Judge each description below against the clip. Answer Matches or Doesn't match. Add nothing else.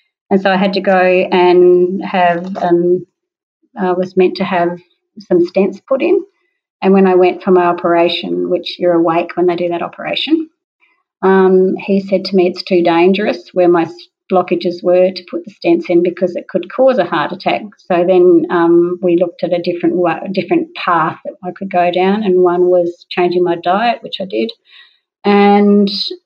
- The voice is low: Doesn't match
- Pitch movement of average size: Doesn't match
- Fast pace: Doesn't match